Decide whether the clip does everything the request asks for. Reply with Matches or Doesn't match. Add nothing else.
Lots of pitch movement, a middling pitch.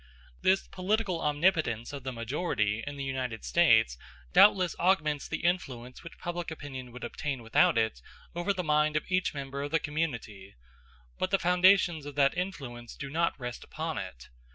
Matches